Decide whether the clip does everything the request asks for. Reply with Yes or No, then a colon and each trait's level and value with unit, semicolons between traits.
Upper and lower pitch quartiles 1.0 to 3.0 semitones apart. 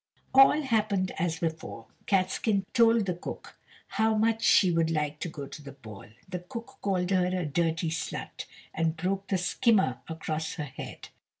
No: average, 4.4 semitones